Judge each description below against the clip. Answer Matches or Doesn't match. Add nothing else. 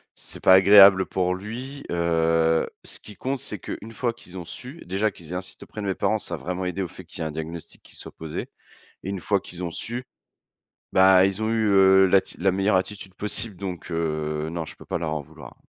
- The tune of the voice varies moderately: Matches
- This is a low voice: Matches